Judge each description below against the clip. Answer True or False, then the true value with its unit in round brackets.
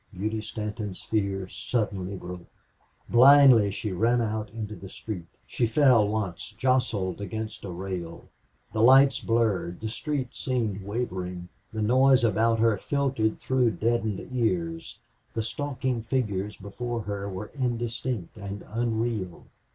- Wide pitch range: False (3.3 semitones)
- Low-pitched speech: True (110 Hz)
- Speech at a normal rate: False (130 wpm)